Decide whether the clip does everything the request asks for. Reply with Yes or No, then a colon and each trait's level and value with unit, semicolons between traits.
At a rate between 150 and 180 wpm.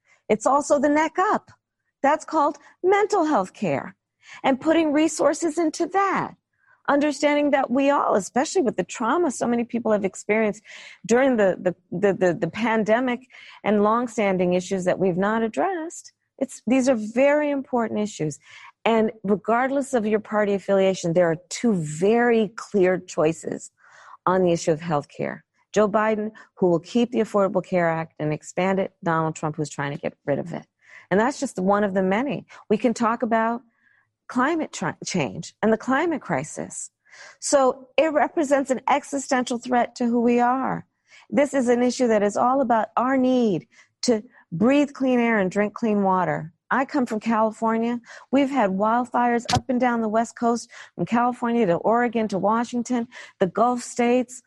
Yes: average, 170 wpm